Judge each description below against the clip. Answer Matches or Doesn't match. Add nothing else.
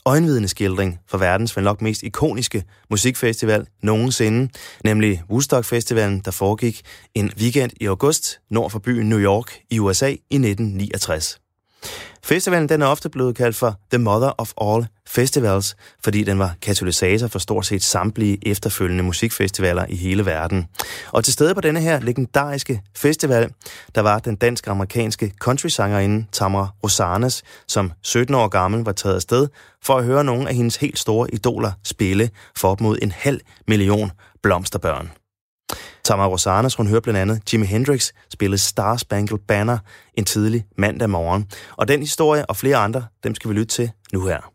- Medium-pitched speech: Doesn't match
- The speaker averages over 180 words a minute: Doesn't match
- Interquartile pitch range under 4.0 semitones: Matches